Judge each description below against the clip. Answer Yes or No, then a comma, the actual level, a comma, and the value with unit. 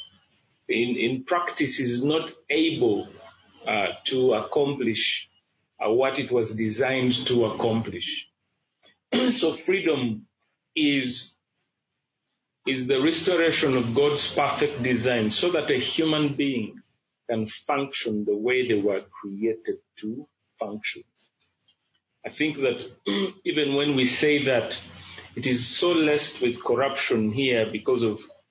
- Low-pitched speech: Yes, low, 130 Hz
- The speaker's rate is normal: No, slow, 120 wpm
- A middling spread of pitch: Yes, average, 4.2 semitones